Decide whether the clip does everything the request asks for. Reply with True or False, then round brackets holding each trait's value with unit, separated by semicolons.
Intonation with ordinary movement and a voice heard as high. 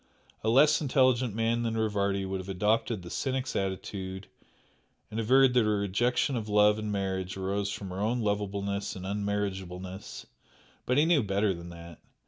False (3.3 semitones; 105 Hz)